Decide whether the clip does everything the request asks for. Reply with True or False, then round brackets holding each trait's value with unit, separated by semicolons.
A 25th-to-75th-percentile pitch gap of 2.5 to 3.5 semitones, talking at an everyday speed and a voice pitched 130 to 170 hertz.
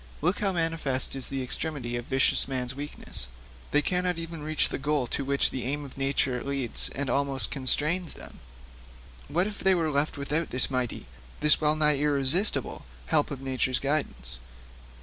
True (2.9 semitones; 170 wpm; 140 Hz)